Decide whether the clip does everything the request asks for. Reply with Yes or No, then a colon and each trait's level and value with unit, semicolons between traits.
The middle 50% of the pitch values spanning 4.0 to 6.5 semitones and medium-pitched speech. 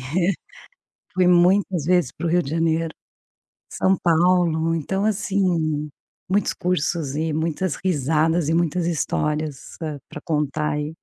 No: average, 2.9 semitones; medium, 165 Hz